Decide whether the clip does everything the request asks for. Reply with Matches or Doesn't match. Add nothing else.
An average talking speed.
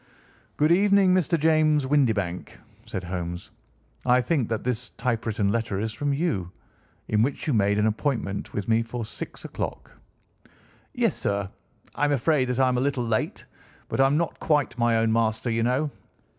Matches